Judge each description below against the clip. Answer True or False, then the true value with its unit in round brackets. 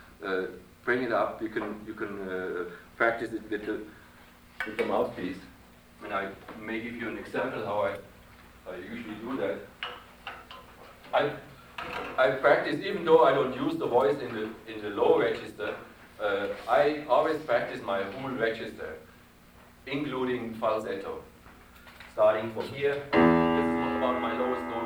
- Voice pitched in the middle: False (110 Hz)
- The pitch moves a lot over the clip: True (8.1 semitones)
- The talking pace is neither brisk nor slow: True (155 wpm)